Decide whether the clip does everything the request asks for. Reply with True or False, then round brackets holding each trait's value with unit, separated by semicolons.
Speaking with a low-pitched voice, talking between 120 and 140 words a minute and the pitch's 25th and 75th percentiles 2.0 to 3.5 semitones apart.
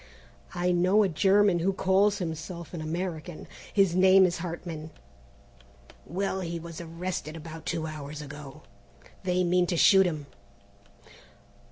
False (175 Hz; 135 wpm; 2.8 semitones)